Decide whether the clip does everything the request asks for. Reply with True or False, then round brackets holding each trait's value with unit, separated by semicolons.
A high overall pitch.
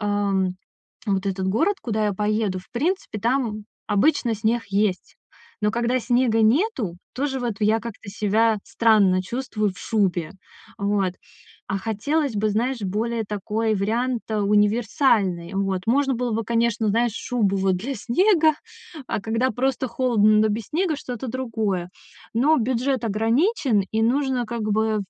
True (220 Hz)